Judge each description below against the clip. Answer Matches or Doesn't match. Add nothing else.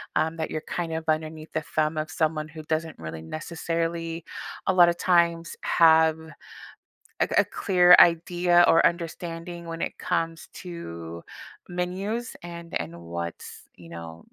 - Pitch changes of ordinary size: Doesn't match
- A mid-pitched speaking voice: Matches